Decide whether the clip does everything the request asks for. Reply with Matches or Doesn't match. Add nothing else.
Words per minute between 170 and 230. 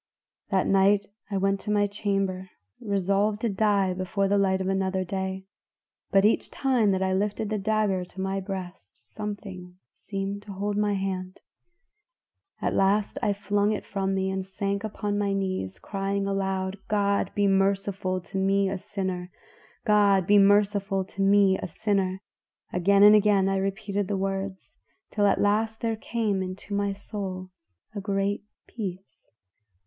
Doesn't match